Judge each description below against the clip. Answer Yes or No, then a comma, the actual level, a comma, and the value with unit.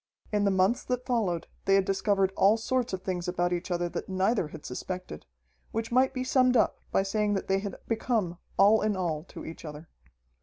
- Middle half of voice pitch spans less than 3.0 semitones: No, average, 4.0 semitones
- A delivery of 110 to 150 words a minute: No, fast, 205 wpm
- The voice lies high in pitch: Yes, high, 195 Hz